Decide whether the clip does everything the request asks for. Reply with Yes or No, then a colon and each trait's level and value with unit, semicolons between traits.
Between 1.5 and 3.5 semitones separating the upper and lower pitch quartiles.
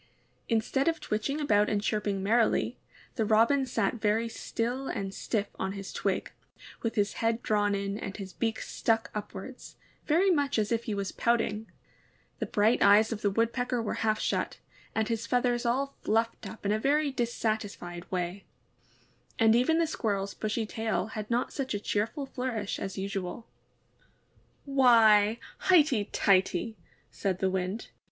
Yes: average, 3.0 semitones